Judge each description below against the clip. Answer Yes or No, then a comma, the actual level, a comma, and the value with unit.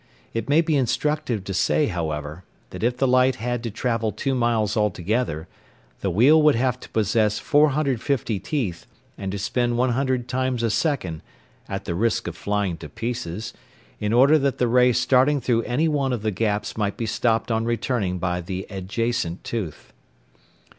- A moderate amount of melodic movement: Yes, average, 4.0 semitones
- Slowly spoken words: No, average, 175 wpm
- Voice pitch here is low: Yes, low, 115 Hz